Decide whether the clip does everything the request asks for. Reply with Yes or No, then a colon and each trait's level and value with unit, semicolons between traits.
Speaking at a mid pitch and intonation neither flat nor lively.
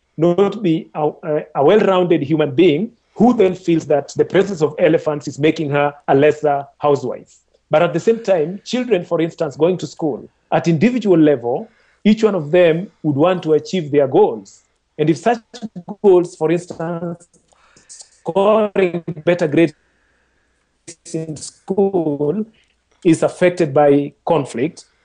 Yes: medium, 170 Hz; average, 4.2 semitones